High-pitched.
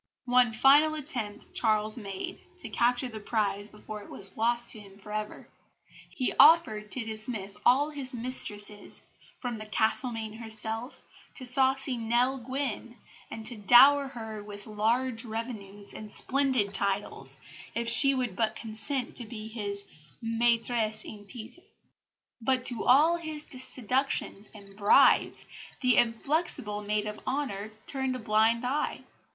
Yes: high, 230 Hz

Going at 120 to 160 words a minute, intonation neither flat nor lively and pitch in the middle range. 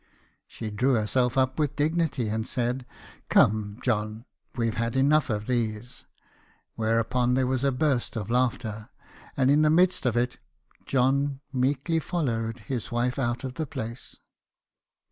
No: average, 150 wpm; average, 3.1 semitones; low, 125 Hz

